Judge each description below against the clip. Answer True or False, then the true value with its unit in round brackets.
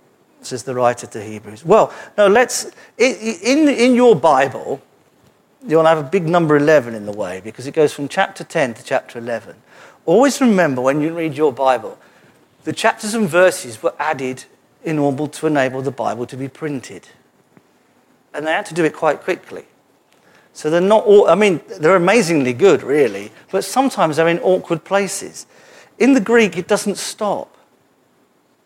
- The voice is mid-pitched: True (165 Hz)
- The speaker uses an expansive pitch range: True (7.3 semitones)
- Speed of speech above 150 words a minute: True (170 wpm)